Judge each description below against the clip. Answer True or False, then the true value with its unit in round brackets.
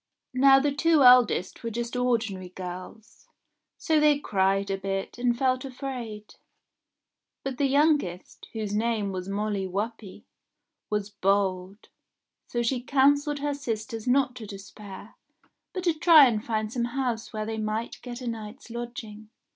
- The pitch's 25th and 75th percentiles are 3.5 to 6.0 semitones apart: True (4.2 semitones)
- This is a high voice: True (230 Hz)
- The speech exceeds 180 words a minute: False (145 wpm)